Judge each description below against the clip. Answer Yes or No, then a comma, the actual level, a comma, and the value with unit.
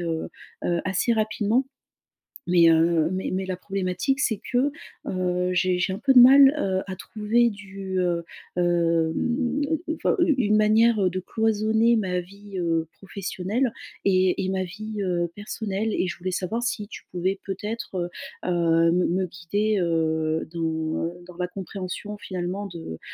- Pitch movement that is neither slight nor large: Yes, average, 3.5 semitones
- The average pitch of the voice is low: No, high, 190 Hz